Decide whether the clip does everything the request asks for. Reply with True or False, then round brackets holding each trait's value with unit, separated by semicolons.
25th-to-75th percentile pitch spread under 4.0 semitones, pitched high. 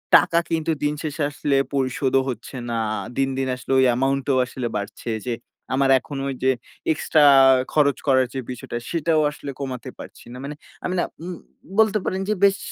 False (2.9 semitones; 140 Hz)